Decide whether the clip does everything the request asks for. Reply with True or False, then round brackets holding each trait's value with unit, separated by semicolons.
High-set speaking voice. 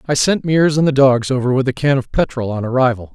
False (130 Hz)